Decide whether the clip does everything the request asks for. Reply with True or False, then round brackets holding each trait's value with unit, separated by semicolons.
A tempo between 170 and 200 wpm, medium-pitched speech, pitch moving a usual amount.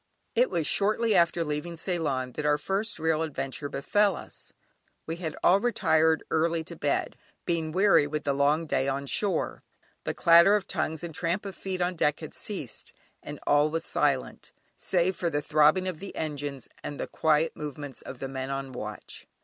True (185 wpm; 160 Hz; 3.4 semitones)